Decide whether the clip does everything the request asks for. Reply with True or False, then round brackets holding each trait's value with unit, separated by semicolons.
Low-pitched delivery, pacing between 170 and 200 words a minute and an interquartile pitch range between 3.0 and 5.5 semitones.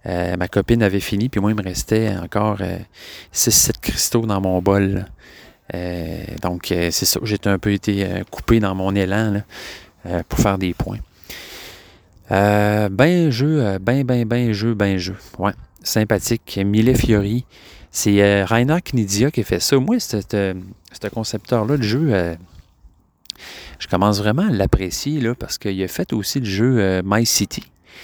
True (100 Hz; 175 wpm; 3.4 semitones)